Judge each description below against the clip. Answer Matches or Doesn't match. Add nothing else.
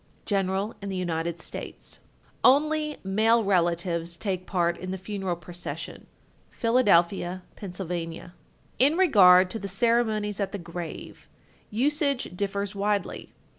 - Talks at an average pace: Doesn't match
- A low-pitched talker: Doesn't match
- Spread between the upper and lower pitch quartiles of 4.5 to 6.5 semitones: Doesn't match